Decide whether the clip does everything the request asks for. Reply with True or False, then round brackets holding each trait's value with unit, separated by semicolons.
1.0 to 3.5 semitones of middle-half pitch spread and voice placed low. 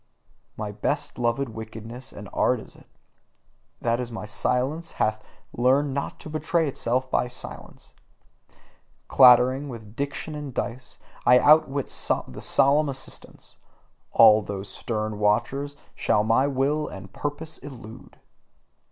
False (4.2 semitones; 125 Hz)